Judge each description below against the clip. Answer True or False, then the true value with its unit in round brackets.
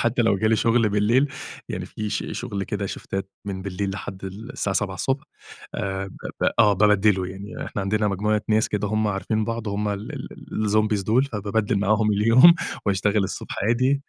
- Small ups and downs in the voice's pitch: True (1.9 semitones)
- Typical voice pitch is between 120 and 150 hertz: False (105 Hz)